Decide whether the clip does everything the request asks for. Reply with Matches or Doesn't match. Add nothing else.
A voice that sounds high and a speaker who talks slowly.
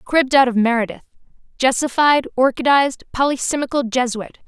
Matches